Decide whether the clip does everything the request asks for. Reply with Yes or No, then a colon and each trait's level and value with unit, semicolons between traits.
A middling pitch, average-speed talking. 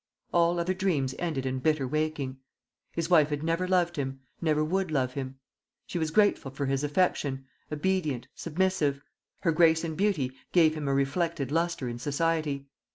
Yes: medium, 155 Hz; average, 165 wpm